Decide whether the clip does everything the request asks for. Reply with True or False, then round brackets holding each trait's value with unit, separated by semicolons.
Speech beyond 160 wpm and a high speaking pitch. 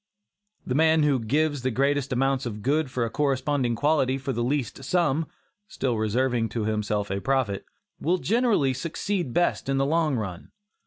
False (170 wpm; 135 Hz)